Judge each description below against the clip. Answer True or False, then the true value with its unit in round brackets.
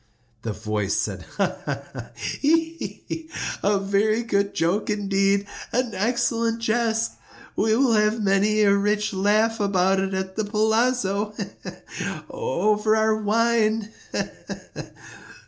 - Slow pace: True (110 wpm)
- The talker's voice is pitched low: False (215 Hz)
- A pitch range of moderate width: False (2.3 semitones)